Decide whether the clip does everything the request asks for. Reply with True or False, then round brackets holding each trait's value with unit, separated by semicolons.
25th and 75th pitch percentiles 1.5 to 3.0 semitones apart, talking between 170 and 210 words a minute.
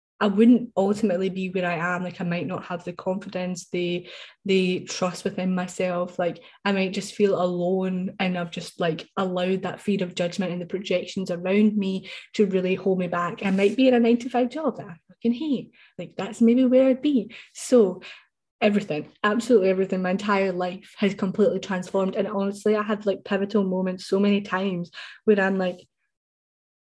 True (2.4 semitones; 190 wpm)